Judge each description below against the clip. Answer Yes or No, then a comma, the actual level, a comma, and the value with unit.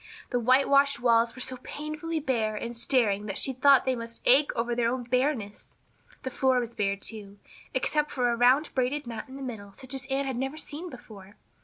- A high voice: Yes, very high, 250 Hz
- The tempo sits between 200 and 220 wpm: Yes, fast, 205 wpm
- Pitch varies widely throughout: No, average, 2.8 semitones